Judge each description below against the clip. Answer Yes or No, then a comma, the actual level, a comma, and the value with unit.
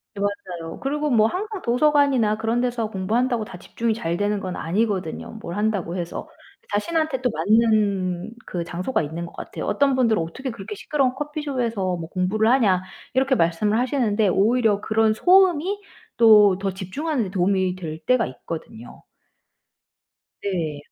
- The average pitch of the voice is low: No, high, 215 Hz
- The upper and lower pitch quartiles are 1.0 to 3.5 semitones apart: No, wide, 5.4 semitones